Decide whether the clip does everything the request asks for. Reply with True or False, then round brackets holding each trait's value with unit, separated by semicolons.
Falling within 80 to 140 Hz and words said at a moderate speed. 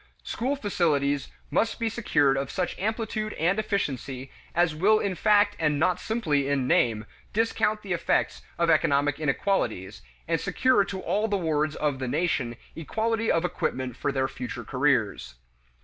False (165 Hz; 155 wpm)